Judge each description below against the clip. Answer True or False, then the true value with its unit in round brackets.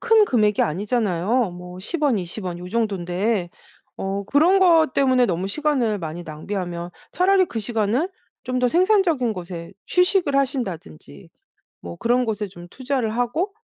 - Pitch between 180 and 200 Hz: False (225 Hz)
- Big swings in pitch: True (7.5 semitones)